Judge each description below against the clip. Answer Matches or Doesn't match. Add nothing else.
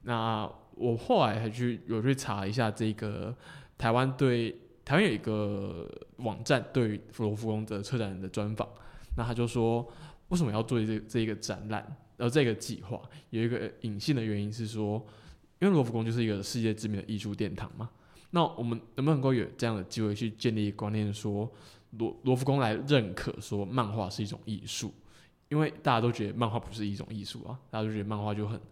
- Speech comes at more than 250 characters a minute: Matches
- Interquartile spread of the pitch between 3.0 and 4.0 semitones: Doesn't match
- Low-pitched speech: Matches